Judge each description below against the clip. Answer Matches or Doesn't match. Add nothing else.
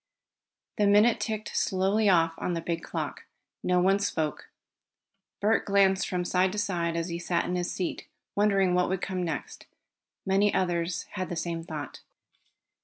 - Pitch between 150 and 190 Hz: Matches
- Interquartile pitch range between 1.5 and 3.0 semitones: Matches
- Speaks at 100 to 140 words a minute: Doesn't match